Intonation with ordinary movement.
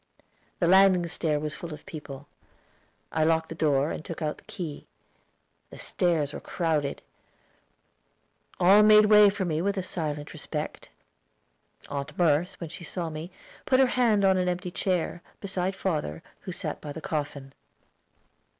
Yes: average, 3.8 semitones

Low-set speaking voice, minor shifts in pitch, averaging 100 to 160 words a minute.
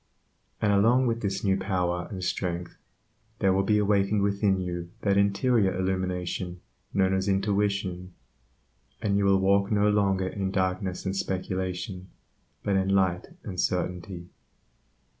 Yes: very low, 95 Hz; narrow, 1.5 semitones; average, 140 wpm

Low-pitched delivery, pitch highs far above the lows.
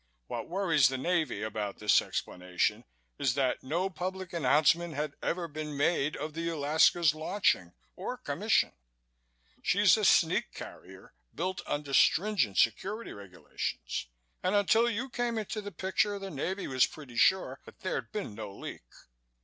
No: medium, 160 Hz; wide, 6.3 semitones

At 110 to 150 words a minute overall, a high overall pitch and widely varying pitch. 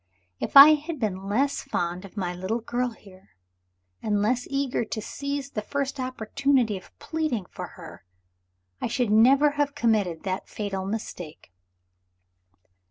Yes: average, 145 wpm; high, 225 Hz; wide, 5.9 semitones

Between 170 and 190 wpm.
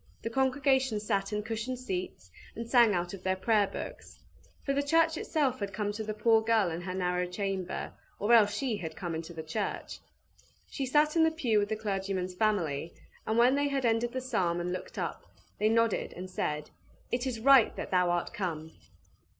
No: average, 200 wpm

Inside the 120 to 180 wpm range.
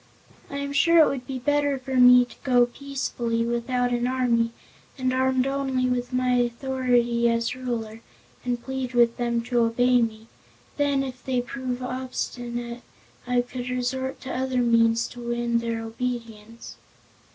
Yes: average, 155 wpm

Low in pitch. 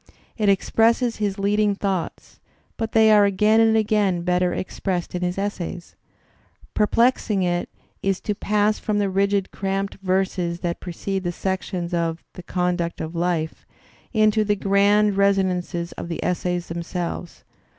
No: high, 195 Hz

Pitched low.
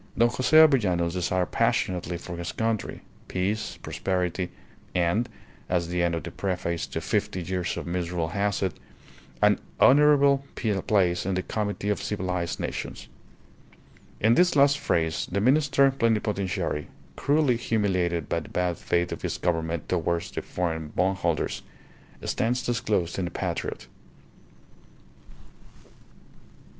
Yes: very low, 95 Hz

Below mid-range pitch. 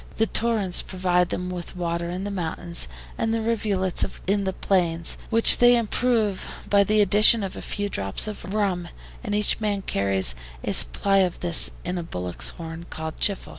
No: high, 190 Hz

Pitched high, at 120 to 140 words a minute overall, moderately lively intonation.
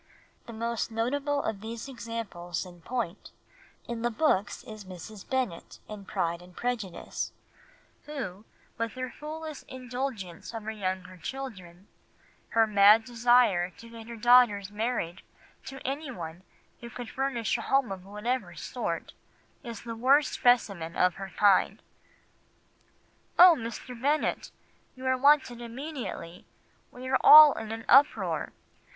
Yes: high, 230 Hz; slow, 135 wpm; average, 4.6 semitones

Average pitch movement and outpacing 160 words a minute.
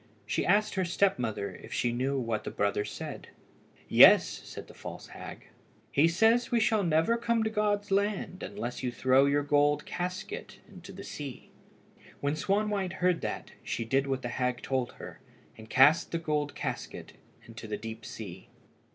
No: wide, 8.0 semitones; average, 175 wpm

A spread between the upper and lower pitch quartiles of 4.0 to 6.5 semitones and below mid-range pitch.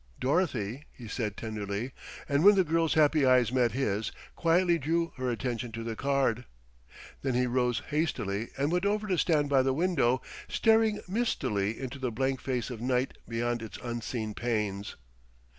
Yes: average, 5.2 semitones; low, 130 Hz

